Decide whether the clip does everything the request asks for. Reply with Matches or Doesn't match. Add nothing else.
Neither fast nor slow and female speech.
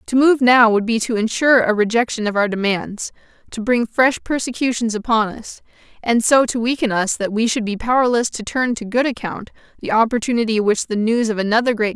Doesn't match